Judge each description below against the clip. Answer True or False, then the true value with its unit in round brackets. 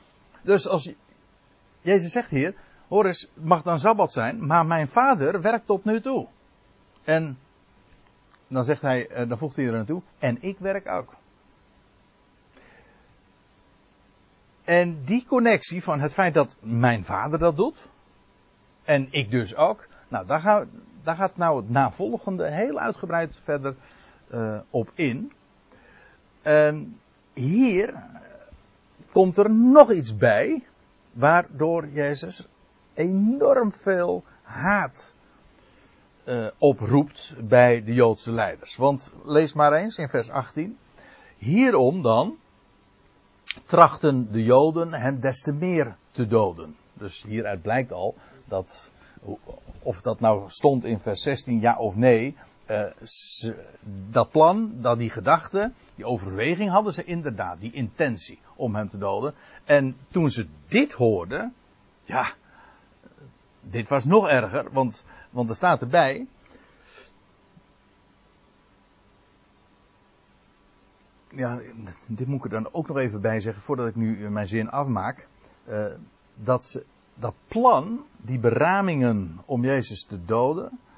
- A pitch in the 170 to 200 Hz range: False (135 Hz)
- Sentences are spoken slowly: True (125 wpm)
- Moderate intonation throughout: False (7.2 semitones)